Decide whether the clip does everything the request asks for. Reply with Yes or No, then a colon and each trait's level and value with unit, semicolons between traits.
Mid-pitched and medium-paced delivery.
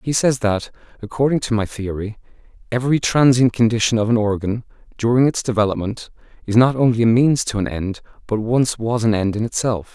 No: low, 115 Hz; average, 185 wpm